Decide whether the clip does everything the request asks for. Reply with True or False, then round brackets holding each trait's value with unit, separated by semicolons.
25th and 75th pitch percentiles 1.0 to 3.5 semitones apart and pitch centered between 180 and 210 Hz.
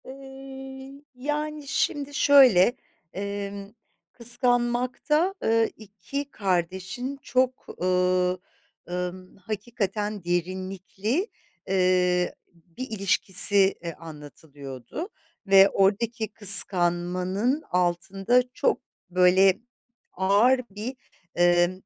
False (5.5 semitones; 200 Hz)